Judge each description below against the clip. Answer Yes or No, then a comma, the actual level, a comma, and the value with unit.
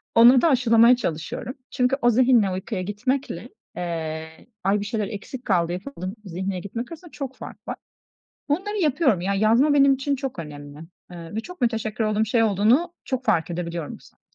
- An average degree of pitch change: No, wide, 6.1 semitones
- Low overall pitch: No, high, 220 Hz